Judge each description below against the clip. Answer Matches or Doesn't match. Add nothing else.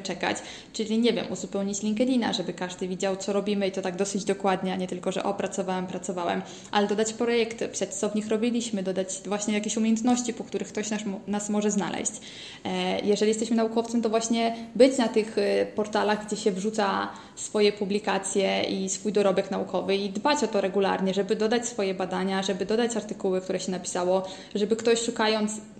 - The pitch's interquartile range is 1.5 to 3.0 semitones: Matches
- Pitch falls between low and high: Doesn't match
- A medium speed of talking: Doesn't match